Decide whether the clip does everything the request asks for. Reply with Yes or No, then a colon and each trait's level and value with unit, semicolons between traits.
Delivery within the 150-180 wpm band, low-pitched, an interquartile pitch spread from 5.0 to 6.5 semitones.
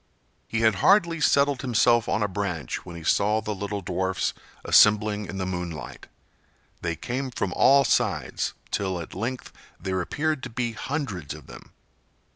Yes: average, 160 wpm; low, 105 Hz; average, 5.3 semitones